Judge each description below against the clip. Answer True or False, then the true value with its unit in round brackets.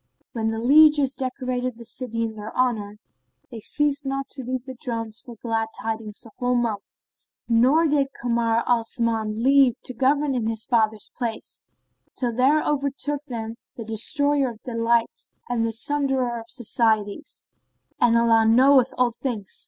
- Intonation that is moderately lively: True (3.0 semitones)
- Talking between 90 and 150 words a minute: False (160 wpm)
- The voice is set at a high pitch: True (240 Hz)